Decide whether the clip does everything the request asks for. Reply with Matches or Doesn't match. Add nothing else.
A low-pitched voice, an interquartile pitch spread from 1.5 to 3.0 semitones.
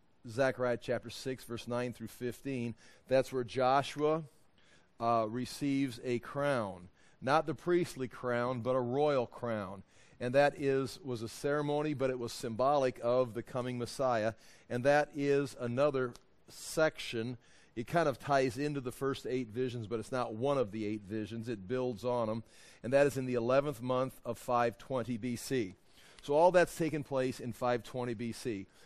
Matches